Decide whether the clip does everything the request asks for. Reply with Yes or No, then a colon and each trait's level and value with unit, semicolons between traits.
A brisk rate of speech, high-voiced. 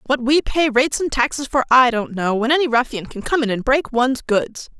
Yes: fast, 250 wpm; very high, 255 Hz